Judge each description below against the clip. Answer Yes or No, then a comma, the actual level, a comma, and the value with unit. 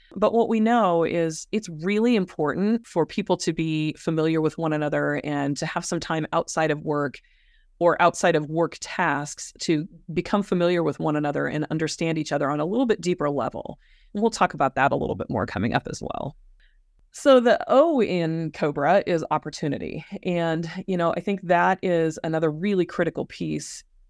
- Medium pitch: Yes, medium, 165 Hz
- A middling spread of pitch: Yes, average, 3.6 semitones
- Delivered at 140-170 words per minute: No, average, 190 wpm